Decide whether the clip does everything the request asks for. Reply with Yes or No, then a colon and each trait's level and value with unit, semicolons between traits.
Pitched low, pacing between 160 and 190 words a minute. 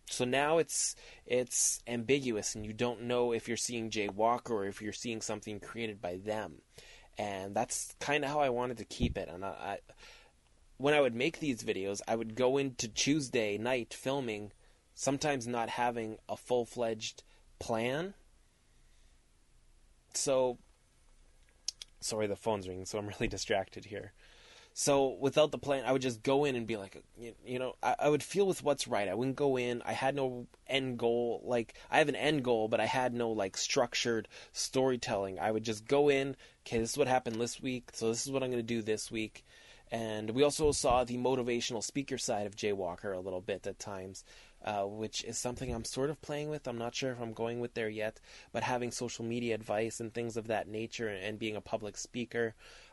No: low, 115 Hz; average, 200 wpm